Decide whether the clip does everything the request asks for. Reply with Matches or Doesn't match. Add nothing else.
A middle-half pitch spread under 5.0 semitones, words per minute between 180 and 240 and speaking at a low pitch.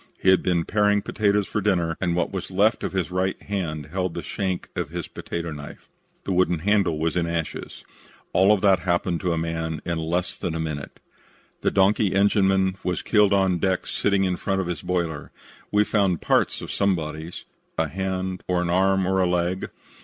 Matches